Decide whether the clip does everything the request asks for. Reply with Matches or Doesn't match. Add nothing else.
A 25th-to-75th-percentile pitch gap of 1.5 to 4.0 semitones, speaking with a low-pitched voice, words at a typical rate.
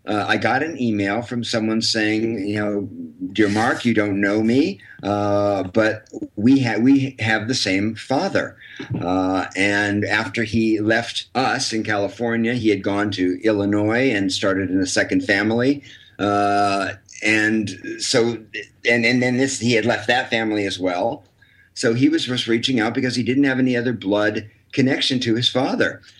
Matches